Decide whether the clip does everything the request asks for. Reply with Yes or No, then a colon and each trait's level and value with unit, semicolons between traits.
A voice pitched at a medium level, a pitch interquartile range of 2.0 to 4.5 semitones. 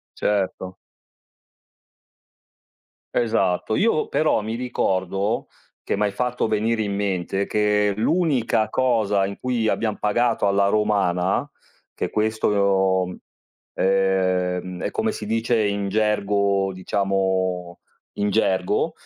No: low, 100 Hz; narrow, 2.4 semitones